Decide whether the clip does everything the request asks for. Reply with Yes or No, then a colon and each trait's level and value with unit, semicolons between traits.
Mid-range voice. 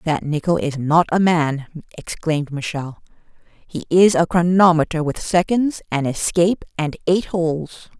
Yes: medium, 165 Hz